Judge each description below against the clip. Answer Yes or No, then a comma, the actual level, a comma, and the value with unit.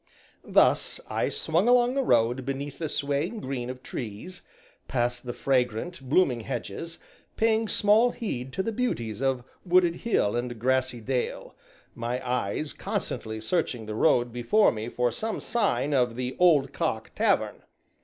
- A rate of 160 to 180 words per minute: No, average, 150 wpm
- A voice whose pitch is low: Yes, low, 130 Hz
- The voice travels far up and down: Yes, wide, 6.8 semitones